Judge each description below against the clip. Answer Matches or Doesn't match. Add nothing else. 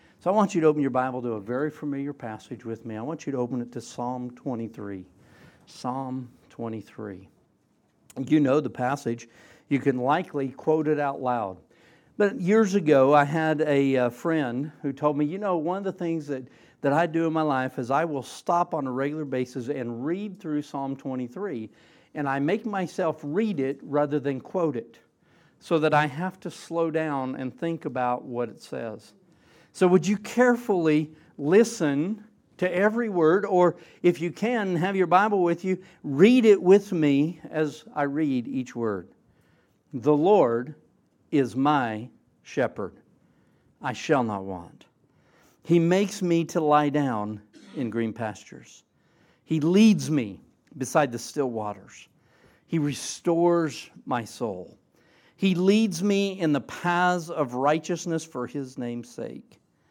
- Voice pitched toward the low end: Doesn't match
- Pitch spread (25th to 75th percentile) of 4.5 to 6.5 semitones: Matches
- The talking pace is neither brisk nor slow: Matches